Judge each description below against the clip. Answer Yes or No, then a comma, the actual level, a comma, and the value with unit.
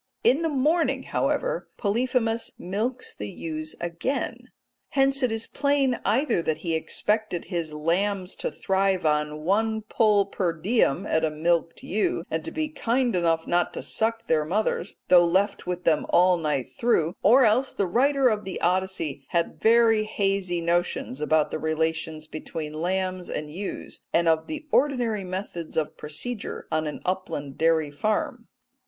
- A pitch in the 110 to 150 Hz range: No, medium, 185 Hz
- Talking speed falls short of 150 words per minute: No, average, 160 wpm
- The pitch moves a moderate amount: No, wide, 5.7 semitones